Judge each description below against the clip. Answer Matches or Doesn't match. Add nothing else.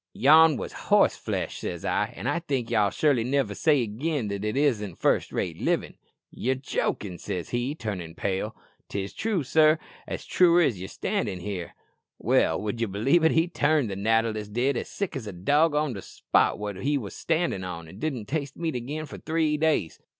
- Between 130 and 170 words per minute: Doesn't match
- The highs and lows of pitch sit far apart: Matches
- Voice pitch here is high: Doesn't match